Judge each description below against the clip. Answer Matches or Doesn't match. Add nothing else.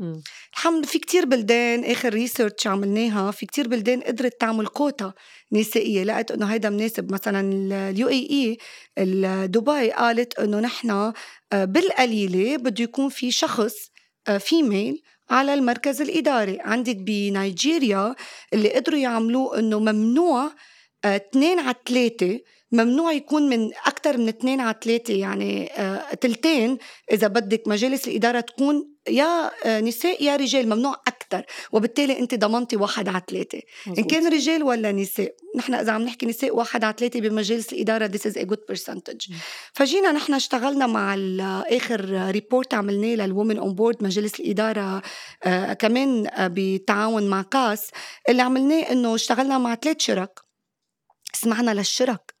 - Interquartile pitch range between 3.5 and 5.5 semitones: Matches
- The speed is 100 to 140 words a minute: Matches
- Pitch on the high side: Matches